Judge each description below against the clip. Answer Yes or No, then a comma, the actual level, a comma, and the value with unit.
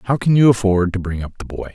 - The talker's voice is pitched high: No, low, 105 Hz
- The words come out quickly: Yes, fast, 310 wpm